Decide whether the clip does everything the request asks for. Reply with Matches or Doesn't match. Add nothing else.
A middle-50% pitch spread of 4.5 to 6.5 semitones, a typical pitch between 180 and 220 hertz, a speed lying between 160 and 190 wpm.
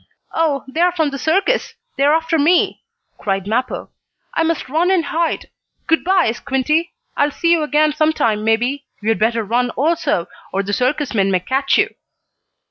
Doesn't match